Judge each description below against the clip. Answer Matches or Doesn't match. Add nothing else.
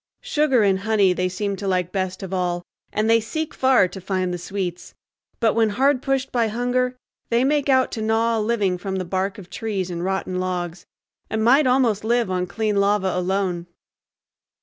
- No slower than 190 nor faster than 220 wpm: Matches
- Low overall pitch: Doesn't match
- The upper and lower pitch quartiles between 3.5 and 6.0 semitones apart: Matches